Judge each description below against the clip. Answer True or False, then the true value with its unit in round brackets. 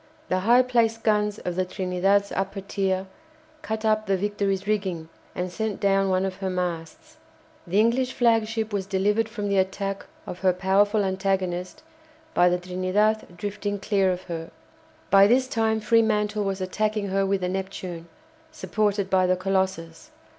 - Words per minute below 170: True (160 wpm)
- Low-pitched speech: False (195 Hz)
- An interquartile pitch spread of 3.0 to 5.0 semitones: False (2.4 semitones)